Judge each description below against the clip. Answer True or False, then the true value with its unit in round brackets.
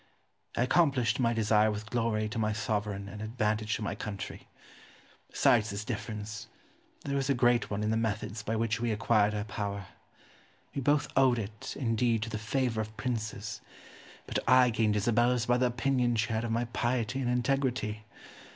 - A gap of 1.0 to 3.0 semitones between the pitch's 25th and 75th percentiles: True (2.4 semitones)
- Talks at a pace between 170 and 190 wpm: True (180 wpm)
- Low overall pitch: True (115 Hz)